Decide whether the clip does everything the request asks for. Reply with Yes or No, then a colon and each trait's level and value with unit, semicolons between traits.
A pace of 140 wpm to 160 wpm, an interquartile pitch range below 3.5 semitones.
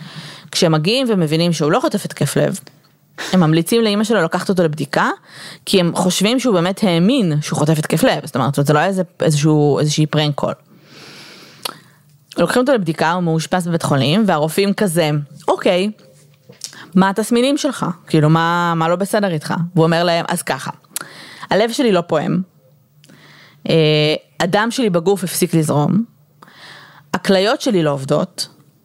No: fast, 150 wpm; average, 4.1 semitones